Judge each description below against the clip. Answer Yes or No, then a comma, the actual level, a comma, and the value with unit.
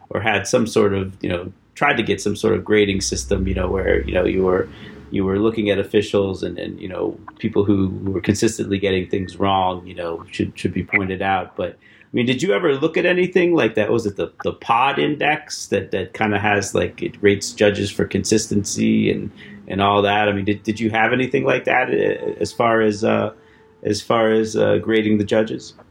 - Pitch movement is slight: Yes, narrow, 2.3 semitones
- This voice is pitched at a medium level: No, low, 105 Hz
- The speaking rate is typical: No, fast, 225 wpm